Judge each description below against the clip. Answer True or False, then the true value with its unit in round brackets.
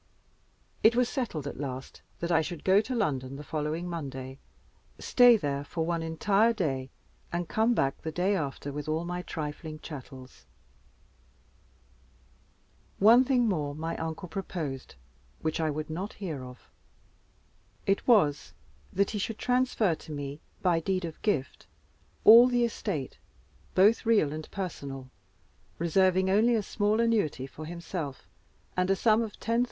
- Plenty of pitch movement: True (6.0 semitones)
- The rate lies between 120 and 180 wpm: True (145 wpm)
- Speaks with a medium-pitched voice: True (170 Hz)